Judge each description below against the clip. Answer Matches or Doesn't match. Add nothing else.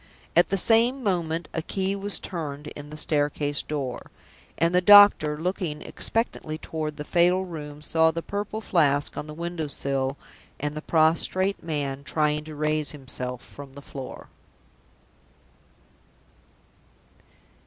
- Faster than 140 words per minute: Doesn't match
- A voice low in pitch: Doesn't match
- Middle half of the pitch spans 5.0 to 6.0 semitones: Doesn't match